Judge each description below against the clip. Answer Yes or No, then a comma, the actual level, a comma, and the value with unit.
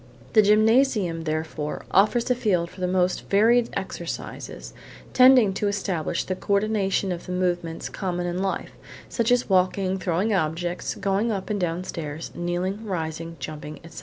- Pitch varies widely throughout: No, average, 3.4 semitones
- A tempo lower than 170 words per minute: Yes, average, 160 wpm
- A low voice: No, medium, 185 Hz